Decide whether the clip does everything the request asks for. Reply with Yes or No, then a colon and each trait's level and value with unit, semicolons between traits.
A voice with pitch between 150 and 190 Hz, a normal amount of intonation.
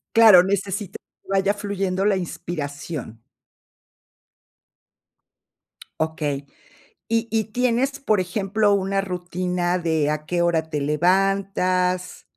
Yes: medium, 185 Hz; average, 3.0 semitones